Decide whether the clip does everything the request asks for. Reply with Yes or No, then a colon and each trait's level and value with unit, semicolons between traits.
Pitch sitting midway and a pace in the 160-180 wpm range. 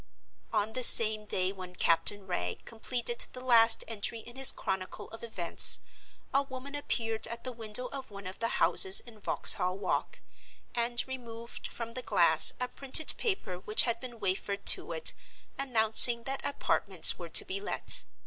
No: high, 230 Hz; average, 170 wpm